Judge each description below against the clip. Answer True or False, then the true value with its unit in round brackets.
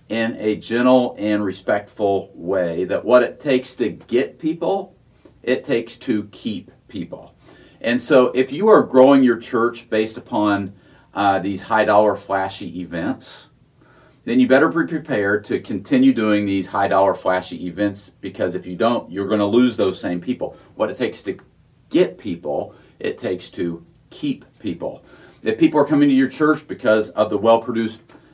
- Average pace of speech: True (170 wpm)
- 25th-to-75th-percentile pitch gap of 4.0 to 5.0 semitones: True (4.4 semitones)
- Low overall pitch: True (110 Hz)